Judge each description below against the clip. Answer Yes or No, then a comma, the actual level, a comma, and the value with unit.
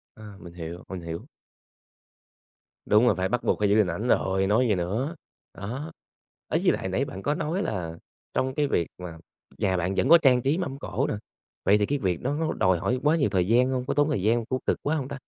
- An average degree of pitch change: No, wide, 6.6 semitones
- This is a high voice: No, low, 110 Hz